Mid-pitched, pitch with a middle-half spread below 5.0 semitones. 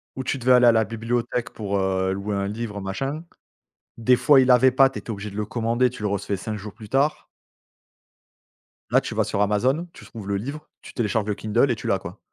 No: low, 110 Hz; average, 3.8 semitones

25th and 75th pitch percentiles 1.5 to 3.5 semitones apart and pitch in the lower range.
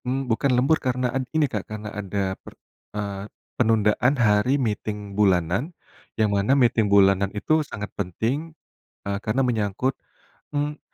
No: average, 4.5 semitones; low, 110 Hz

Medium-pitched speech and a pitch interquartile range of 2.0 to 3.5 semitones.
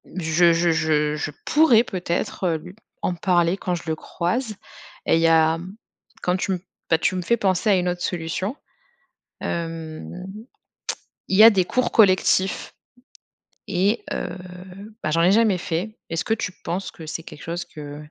Yes: medium, 175 Hz; average, 2.9 semitones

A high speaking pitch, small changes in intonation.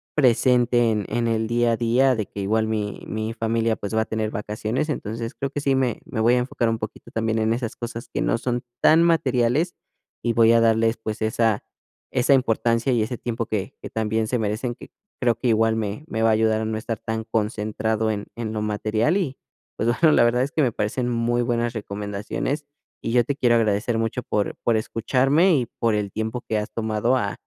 No: low, 115 Hz; narrow, 2.0 semitones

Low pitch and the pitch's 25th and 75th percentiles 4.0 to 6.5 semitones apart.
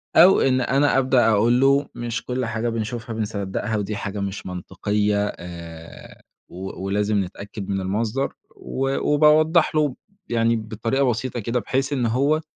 Yes: low, 115 Hz; average, 4.6 semitones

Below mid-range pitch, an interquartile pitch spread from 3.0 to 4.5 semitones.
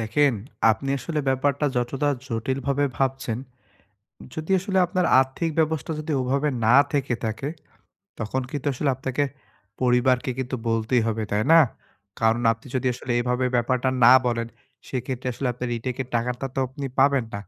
No: low, 130 Hz; narrow, 2.6 semitones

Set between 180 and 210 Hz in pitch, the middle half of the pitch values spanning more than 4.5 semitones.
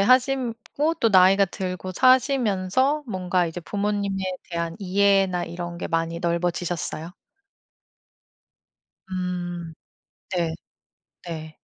No: medium, 185 Hz; average, 3.2 semitones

